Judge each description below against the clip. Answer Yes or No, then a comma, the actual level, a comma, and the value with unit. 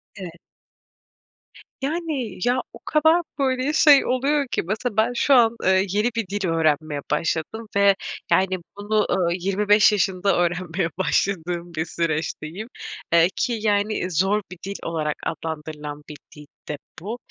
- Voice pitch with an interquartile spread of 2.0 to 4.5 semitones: No, average, 5.3 semitones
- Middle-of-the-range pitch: No, high, 195 Hz